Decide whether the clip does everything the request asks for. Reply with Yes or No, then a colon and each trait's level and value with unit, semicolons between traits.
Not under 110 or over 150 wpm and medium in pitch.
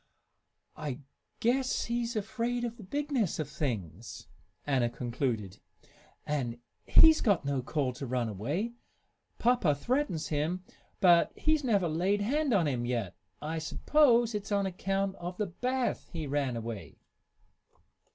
Yes: slow, 135 wpm; medium, 175 Hz